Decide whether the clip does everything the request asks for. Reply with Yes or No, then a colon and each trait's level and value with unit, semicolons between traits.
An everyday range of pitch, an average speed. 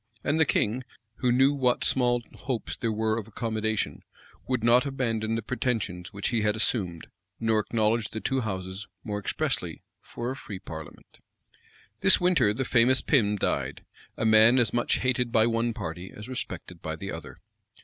Yes: average, 3.1 semitones; average, 175 wpm